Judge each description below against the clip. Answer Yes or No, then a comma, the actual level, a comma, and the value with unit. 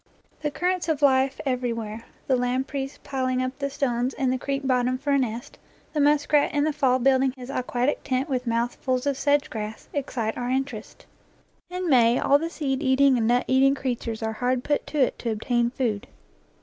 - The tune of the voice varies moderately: No, narrow, 2.2 semitones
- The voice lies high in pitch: Yes, very high, 260 Hz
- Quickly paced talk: No, average, 195 wpm